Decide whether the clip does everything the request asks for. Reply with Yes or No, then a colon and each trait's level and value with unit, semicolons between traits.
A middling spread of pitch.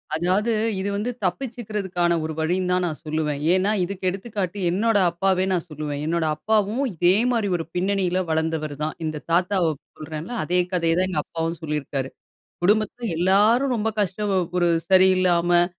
Yes: average, 3.7 semitones